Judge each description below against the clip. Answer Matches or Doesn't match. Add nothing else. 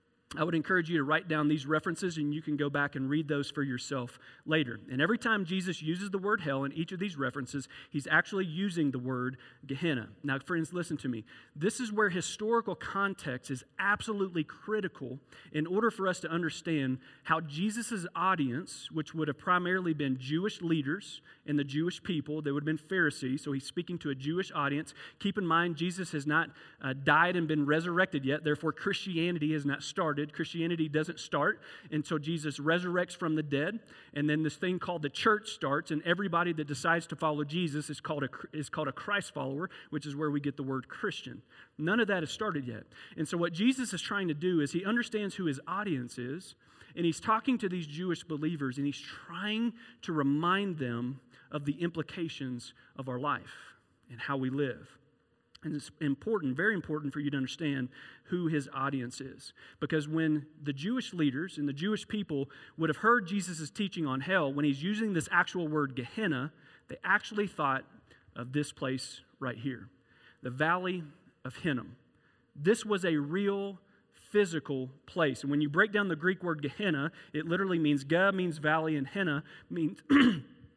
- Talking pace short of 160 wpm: Doesn't match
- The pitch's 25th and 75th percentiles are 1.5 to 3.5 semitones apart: Doesn't match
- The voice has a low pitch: Doesn't match